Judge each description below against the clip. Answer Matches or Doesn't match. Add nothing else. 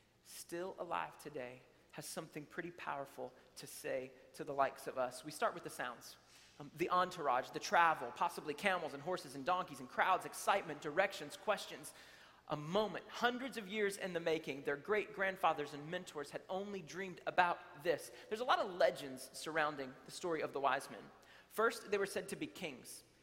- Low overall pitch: Doesn't match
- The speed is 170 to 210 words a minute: Matches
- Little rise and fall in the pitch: Doesn't match